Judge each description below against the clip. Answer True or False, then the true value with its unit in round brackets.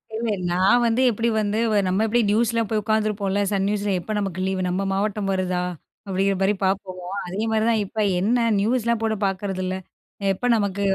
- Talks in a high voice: True (205 Hz)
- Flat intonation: True (2.3 semitones)